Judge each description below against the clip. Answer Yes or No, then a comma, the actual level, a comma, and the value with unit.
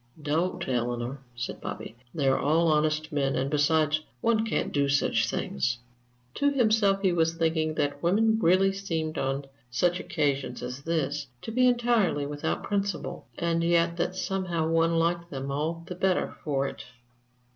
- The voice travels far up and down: No, average, 4.3 semitones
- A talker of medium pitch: Yes, medium, 165 Hz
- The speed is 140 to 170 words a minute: Yes, average, 155 wpm